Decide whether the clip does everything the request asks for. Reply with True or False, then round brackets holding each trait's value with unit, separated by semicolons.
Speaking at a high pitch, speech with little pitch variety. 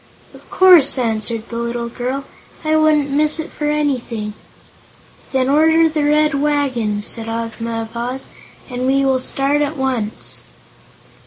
False (265 Hz; 4.2 semitones)